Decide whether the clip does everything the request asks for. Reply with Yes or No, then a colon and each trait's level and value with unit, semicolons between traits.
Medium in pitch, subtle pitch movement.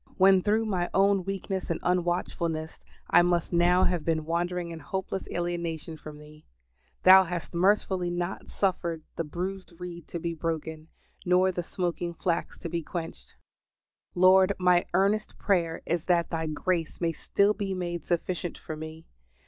Yes: medium, 175 Hz; narrow, 2.0 semitones